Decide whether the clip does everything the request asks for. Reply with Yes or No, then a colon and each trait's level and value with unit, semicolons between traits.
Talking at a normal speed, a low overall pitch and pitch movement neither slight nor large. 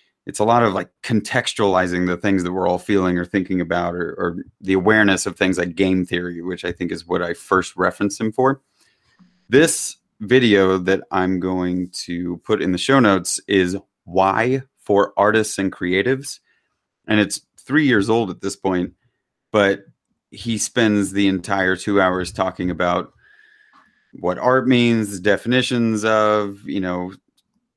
Yes: average, 160 wpm; very low, 95 Hz; average, 3.0 semitones